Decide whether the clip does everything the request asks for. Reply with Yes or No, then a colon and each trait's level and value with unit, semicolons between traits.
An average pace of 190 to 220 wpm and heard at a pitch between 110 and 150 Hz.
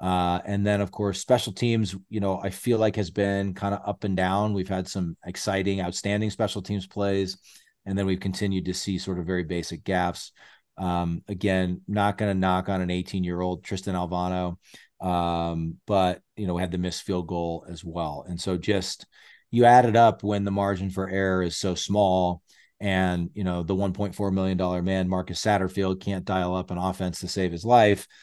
No: average, 200 wpm; very low, 95 Hz